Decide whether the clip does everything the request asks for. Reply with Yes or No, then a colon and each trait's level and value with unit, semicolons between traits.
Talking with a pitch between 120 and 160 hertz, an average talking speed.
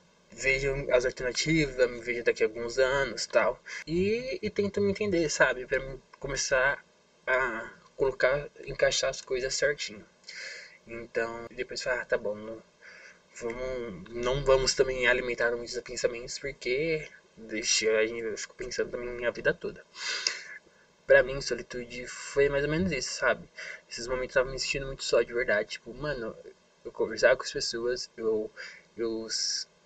Yes: low, 135 Hz; average, 150 wpm